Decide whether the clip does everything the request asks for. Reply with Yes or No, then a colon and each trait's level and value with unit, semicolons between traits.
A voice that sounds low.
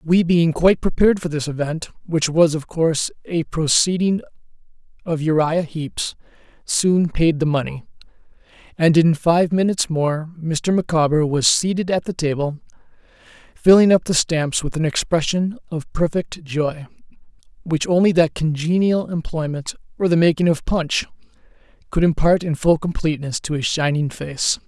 No: medium, 165 Hz